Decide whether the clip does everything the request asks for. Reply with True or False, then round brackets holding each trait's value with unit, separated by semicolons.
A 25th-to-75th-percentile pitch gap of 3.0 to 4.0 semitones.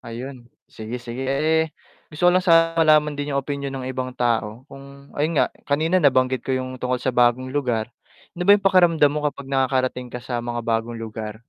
True (3.7 semitones)